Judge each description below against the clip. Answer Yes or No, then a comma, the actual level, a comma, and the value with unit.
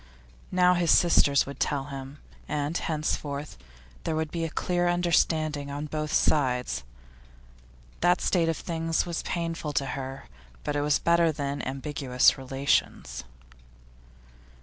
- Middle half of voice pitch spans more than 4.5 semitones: No, average, 3.0 semitones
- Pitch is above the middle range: No, medium, 150 Hz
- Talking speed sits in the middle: No, slow, 130 wpm